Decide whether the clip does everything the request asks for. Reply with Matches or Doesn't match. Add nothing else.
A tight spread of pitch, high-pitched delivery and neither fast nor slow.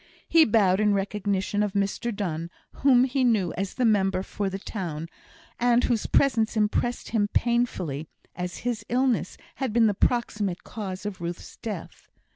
Doesn't match